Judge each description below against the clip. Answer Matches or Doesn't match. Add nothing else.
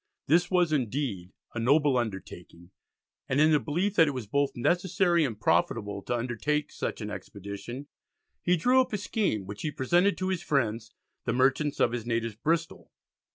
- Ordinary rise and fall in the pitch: Doesn't match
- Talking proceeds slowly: Doesn't match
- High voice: Doesn't match